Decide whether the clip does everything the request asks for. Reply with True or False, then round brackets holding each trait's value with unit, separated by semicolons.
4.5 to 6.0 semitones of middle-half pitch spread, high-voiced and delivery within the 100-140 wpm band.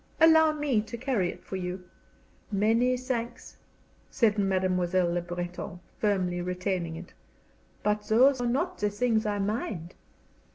True (5.1 semitones; 205 Hz; 135 wpm)